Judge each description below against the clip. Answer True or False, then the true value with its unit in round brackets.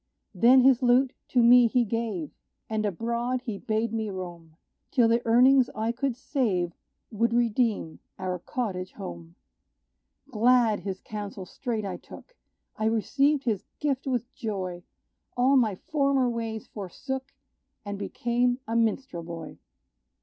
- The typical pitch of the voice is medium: False (230 Hz)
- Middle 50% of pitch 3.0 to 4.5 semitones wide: True (3.9 semitones)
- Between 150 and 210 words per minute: False (135 wpm)